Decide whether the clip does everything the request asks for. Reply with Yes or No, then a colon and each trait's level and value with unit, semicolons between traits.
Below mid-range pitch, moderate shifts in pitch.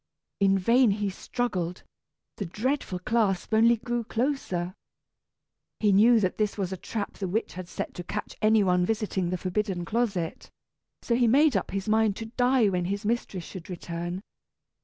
No: high, 205 Hz; average, 4.0 semitones